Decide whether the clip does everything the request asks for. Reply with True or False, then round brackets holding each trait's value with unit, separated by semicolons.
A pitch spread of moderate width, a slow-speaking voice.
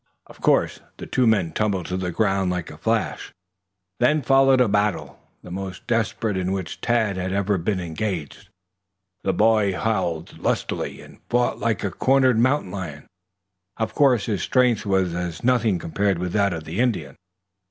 False (4.3 semitones; 170 wpm)